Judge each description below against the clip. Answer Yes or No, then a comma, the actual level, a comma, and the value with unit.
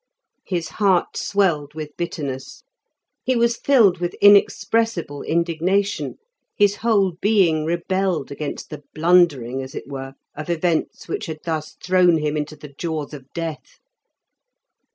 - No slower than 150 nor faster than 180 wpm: No, slow, 135 wpm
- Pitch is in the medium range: Yes, medium, 170 Hz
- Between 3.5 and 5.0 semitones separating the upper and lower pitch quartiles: Yes, average, 4.2 semitones